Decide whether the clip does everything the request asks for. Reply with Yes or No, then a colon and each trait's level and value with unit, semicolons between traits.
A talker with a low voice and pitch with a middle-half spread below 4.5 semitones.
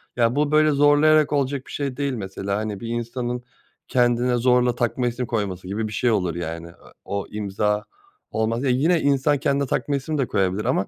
No: low, 120 Hz; average, 5.0 semitones